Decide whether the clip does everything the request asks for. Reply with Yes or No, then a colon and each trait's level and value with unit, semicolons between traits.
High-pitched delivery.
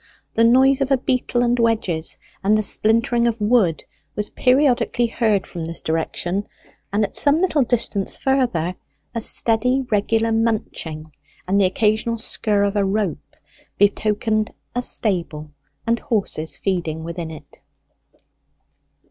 Yes: high, 215 Hz